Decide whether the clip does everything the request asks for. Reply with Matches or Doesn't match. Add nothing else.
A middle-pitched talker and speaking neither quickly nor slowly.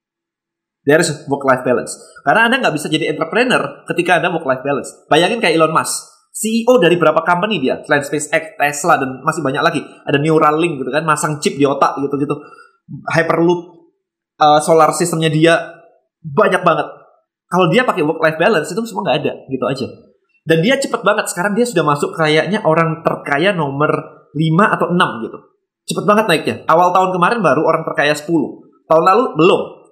Doesn't match